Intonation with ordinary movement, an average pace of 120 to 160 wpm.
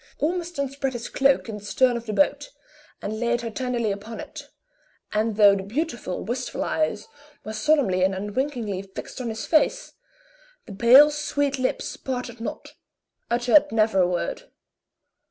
Yes: average, 4.7 semitones; average, 155 wpm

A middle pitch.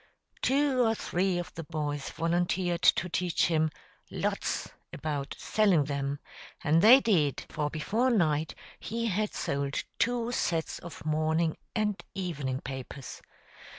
Yes: medium, 170 Hz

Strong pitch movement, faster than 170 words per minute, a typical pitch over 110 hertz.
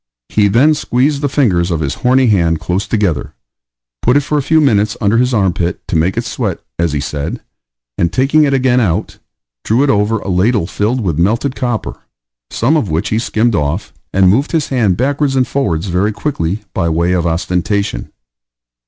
No: wide, 6.7 semitones; average, 190 wpm; low, 105 Hz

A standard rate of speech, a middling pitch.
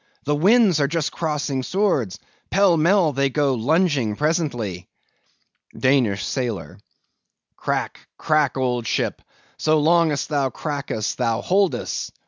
No: slow, 120 wpm; medium, 145 Hz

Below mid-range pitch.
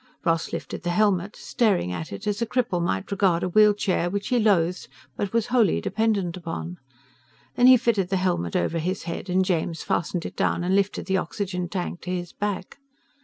No: medium, 185 Hz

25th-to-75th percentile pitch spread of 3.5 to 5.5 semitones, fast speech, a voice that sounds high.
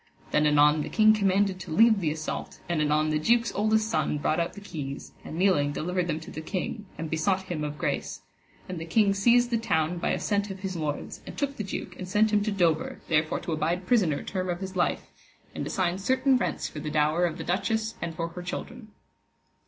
No: average, 4.7 semitones; fast, 225 wpm; medium, 180 Hz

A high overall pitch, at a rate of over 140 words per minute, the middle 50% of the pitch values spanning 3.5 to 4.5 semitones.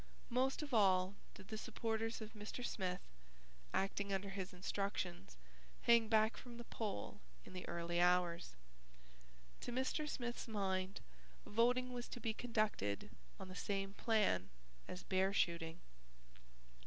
No: high, 200 Hz; slow, 135 wpm; average, 4.1 semitones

